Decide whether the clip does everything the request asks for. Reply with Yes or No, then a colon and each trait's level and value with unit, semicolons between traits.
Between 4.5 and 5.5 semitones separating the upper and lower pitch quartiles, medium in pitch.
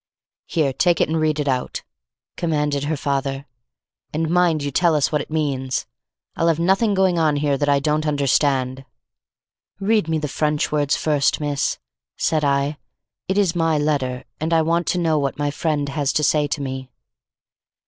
No: narrow, 2.4 semitones; medium, 150 Hz